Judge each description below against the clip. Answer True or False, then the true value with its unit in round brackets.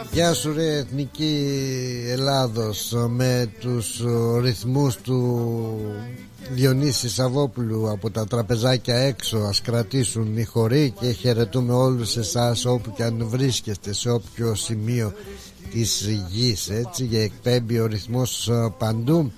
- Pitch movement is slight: True (2.2 semitones)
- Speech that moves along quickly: False (115 wpm)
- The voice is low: True (120 Hz)